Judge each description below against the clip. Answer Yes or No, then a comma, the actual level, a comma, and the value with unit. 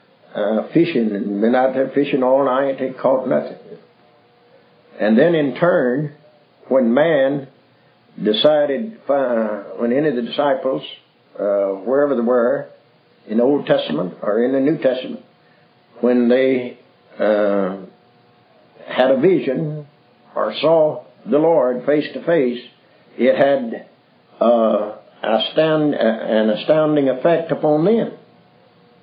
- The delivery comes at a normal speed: No, slow, 130 wpm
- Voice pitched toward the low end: Yes, low, 130 Hz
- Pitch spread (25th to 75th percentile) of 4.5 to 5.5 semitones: No, average, 4.0 semitones